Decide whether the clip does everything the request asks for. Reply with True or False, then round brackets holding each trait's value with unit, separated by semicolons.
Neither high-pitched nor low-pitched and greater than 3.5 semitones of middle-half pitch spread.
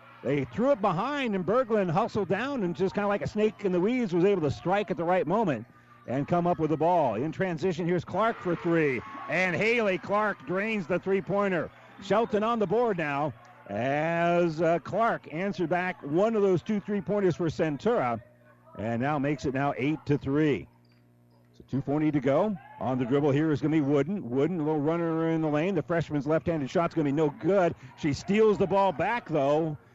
True (170 Hz; 5.1 semitones)